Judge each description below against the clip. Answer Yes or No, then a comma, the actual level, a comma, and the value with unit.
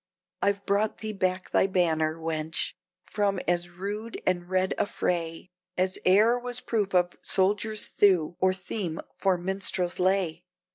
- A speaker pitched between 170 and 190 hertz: Yes, medium, 185 Hz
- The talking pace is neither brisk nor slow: Yes, average, 145 wpm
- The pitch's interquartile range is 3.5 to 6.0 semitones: No, narrow, 2.5 semitones